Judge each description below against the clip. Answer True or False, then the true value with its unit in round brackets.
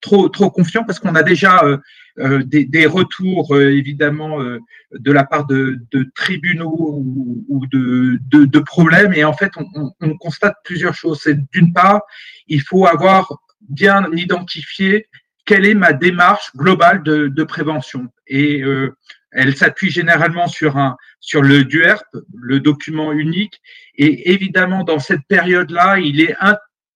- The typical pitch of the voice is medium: True (160 Hz)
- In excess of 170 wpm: False (165 wpm)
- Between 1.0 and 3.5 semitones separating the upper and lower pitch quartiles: False (4.4 semitones)